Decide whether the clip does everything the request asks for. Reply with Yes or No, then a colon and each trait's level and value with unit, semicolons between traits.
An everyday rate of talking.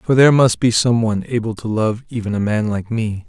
No: fast, 255 wpm